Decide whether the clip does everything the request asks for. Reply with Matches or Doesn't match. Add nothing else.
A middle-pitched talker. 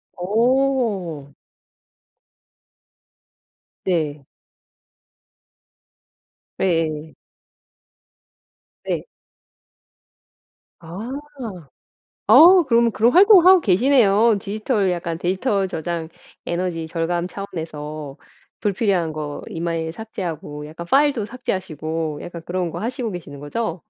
Matches